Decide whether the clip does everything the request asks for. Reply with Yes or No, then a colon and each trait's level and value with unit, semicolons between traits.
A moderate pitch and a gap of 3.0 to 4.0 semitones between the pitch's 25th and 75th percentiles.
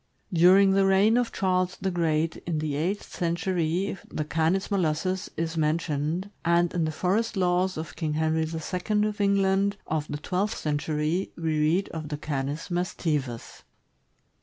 Yes: medium, 170 Hz; average, 3.5 semitones